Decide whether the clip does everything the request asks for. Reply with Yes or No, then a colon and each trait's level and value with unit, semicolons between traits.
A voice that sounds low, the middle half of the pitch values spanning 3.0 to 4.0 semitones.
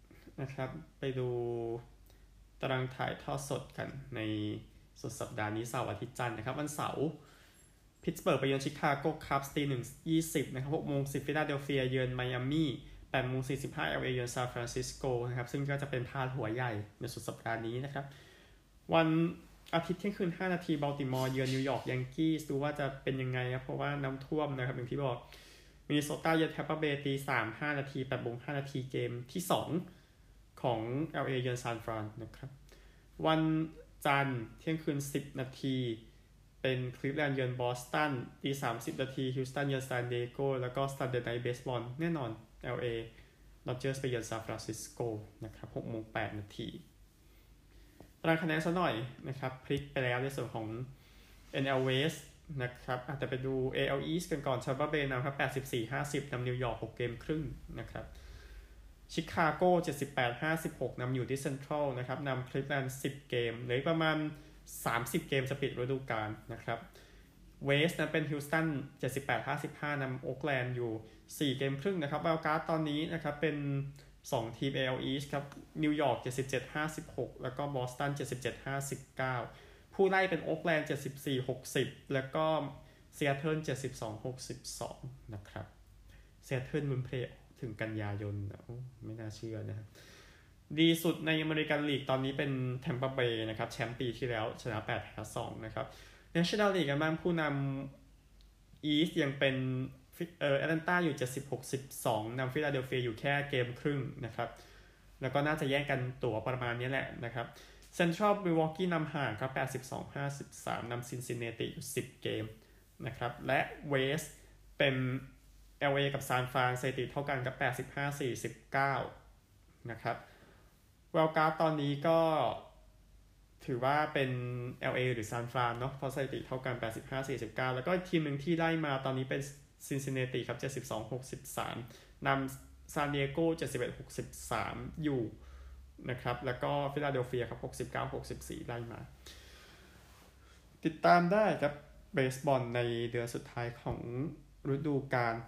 Yes: low, 130 Hz; average, 3.3 semitones